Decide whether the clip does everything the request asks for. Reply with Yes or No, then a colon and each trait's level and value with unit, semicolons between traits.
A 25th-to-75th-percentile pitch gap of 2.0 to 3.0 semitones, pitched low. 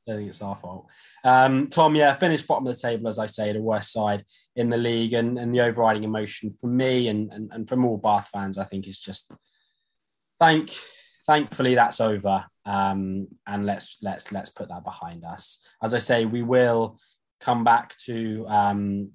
No: average, 3.4 semitones; low, 110 Hz